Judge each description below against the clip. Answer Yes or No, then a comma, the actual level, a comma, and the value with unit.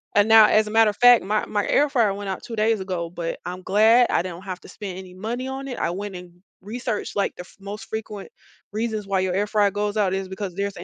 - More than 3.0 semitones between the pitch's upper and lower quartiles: No, average, 2.7 semitones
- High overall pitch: Yes, high, 205 Hz